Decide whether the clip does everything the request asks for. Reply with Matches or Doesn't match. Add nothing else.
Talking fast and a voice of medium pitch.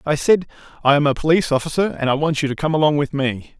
Matches